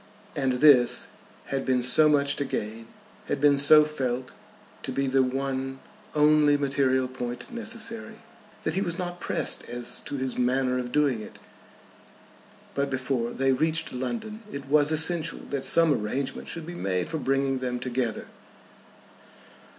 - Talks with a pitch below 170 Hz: Yes, low, 135 Hz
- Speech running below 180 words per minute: Yes, average, 150 wpm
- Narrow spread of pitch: No, average, 3.1 semitones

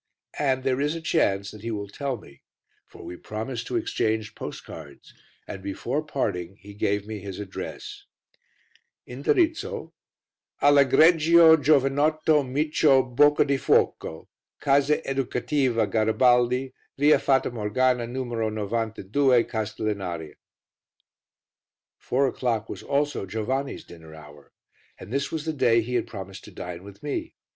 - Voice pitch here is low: Yes, low, 125 Hz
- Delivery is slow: Yes, slow, 125 wpm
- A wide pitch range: Yes, wide, 5.7 semitones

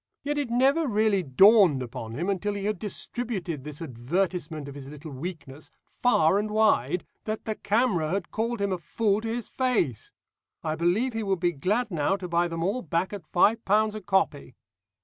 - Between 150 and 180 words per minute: No, average, 190 wpm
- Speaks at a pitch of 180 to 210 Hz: Yes, high, 190 Hz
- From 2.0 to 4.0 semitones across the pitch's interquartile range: No, average, 5.2 semitones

